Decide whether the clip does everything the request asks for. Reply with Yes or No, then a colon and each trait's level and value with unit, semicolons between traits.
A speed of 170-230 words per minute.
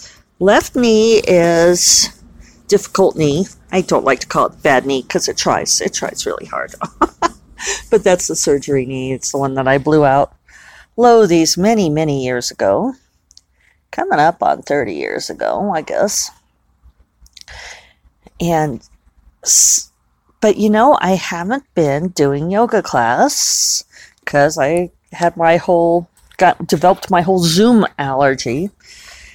No: slow, 135 wpm